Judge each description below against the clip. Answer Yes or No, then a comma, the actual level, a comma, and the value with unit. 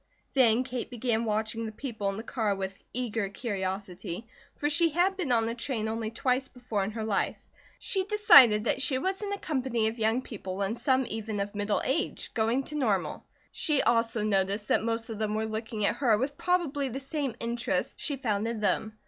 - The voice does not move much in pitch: No, average, 3.8 semitones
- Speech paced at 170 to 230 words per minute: Yes, fast, 205 wpm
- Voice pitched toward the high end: Yes, high, 230 Hz